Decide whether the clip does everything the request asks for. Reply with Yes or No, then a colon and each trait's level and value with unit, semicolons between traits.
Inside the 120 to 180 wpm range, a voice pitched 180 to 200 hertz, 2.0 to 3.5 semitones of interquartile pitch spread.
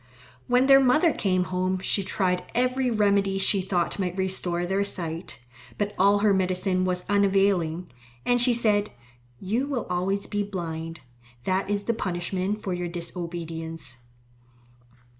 Yes: average, 140 wpm; high, 190 Hz; narrow, 2.5 semitones